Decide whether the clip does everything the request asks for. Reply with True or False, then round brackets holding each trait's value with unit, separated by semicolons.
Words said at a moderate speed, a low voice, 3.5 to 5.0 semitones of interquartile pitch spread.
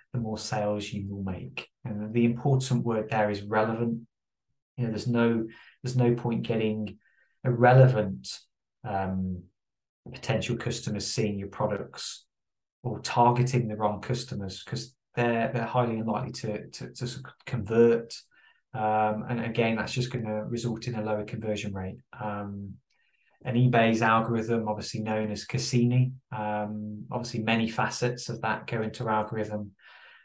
False (145 wpm; 115 Hz; 2.5 semitones)